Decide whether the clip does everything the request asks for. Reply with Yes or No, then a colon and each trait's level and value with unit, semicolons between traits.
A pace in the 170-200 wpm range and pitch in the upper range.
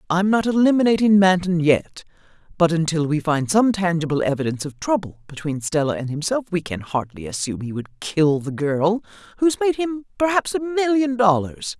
No: average, 175 wpm; medium, 180 Hz